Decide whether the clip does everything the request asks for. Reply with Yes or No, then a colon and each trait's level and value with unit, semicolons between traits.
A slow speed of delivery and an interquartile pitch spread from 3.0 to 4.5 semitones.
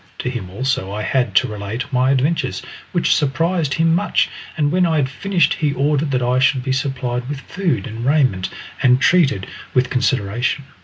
No: average, 185 wpm; average, 3.3 semitones